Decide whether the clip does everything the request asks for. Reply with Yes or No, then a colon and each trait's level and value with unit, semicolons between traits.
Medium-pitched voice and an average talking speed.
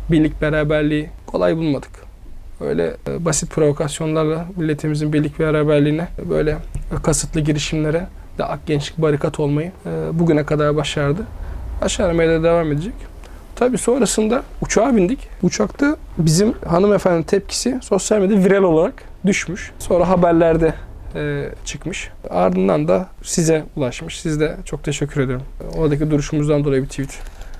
Yes: medium, 155 Hz; average, 130 wpm